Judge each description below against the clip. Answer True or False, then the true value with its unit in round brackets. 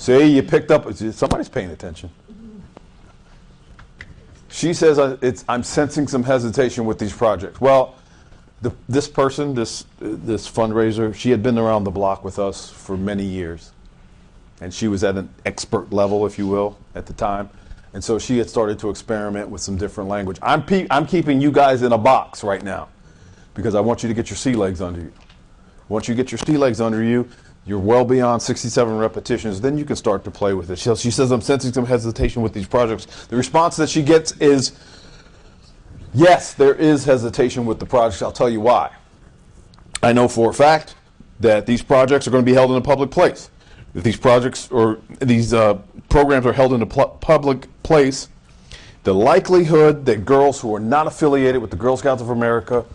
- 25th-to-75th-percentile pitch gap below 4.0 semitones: False (4.6 semitones)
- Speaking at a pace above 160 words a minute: True (195 wpm)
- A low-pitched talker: True (120 Hz)